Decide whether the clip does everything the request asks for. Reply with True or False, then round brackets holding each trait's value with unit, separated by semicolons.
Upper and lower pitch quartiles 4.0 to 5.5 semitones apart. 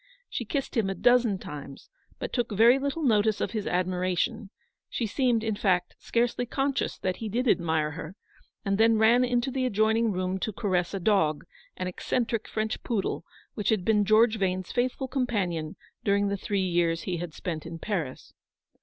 True (4.4 semitones)